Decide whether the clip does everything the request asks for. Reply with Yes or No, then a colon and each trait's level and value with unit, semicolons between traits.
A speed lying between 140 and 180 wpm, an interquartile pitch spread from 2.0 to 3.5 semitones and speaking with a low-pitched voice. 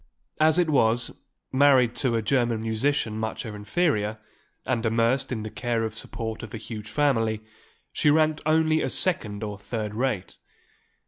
No: average, 165 wpm; average, 4.4 semitones; low, 115 Hz